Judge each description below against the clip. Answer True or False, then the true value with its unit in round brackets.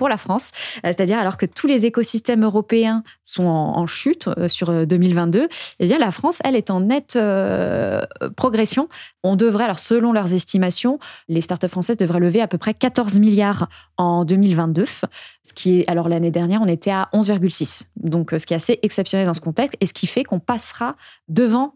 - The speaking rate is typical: True (195 wpm)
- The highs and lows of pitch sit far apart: False (4.9 semitones)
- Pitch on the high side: True (200 Hz)